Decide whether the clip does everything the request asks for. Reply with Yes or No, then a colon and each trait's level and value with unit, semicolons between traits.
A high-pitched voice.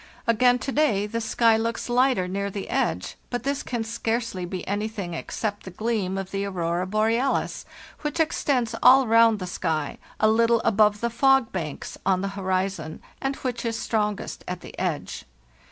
Yes: high, 220 Hz